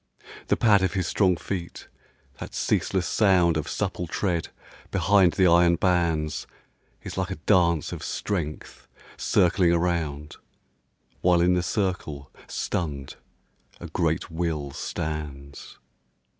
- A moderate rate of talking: No, slow, 120 wpm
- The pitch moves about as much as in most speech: Yes, average, 3.0 semitones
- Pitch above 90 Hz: No, very low, 85 Hz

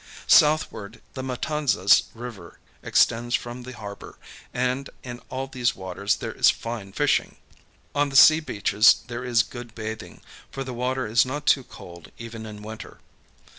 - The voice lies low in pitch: Yes, low, 120 Hz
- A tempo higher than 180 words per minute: No, average, 155 wpm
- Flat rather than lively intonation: No, average, 3.2 semitones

